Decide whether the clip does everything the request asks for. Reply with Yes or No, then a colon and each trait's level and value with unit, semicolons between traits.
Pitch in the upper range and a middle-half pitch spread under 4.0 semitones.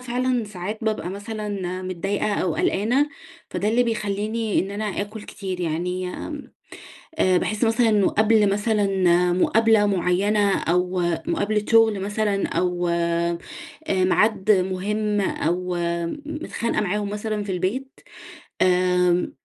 Yes: high, 205 Hz; average, 3.0 semitones